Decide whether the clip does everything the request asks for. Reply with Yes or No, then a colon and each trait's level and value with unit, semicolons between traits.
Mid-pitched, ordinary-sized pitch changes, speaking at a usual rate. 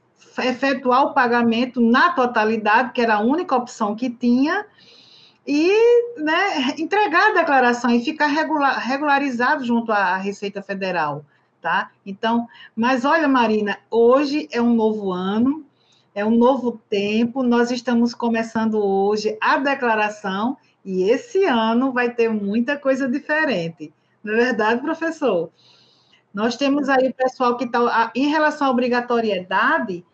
No: high, 245 Hz; average, 4.1 semitones; average, 130 wpm